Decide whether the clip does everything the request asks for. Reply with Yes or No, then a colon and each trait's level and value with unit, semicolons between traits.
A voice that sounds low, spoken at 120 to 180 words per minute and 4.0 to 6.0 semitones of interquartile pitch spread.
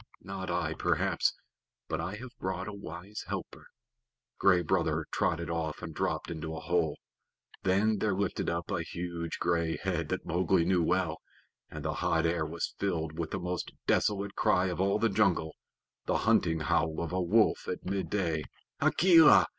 No: very low, 90 Hz; average, 170 wpm; average, 2.8 semitones